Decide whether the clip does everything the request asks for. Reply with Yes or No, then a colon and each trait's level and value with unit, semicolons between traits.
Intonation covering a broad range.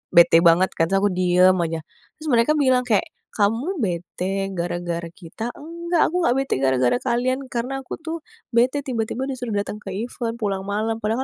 Yes: wide, 6.0 semitones